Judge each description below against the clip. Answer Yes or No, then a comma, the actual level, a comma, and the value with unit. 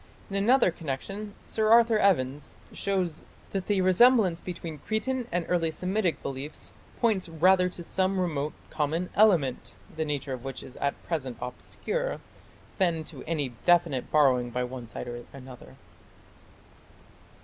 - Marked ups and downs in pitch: Yes, wide, 5.9 semitones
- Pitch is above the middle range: No, medium, 170 Hz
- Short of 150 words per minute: Yes, average, 140 wpm